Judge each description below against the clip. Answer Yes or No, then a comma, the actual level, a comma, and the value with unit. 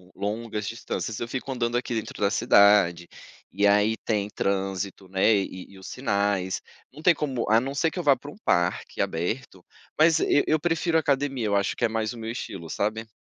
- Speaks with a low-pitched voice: Yes, low, 110 Hz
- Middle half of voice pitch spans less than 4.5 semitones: No, average, 4.8 semitones